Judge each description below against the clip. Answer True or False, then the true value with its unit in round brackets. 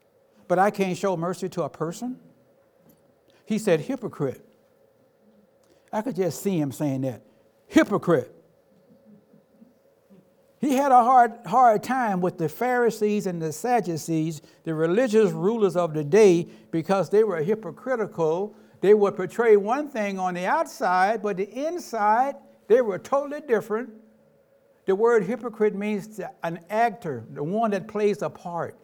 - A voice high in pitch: True (210 Hz)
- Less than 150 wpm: True (140 wpm)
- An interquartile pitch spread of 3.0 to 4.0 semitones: False (5.4 semitones)